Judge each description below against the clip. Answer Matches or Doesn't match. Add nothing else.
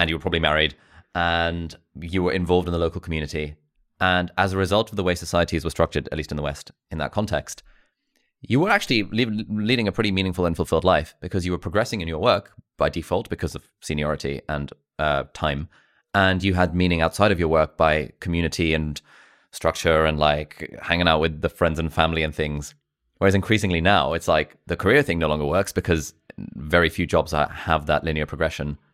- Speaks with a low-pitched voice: Matches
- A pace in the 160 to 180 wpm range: Doesn't match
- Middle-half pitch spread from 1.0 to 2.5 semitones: Doesn't match